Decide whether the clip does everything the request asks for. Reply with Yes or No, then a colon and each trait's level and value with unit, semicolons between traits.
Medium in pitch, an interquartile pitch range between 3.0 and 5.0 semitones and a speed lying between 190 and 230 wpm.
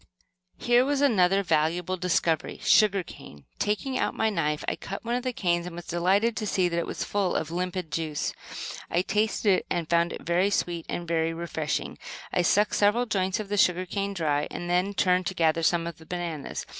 Yes: medium, 180 Hz; average, 3.3 semitones; fast, 205 wpm